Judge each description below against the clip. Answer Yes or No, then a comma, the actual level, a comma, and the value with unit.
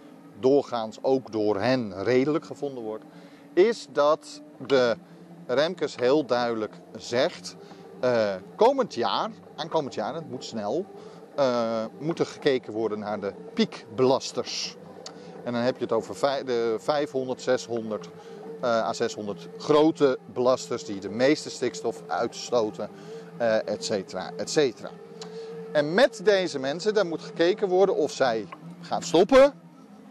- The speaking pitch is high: No, low, 135 Hz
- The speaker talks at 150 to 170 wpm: No, slow, 135 wpm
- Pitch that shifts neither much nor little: No, wide, 6.5 semitones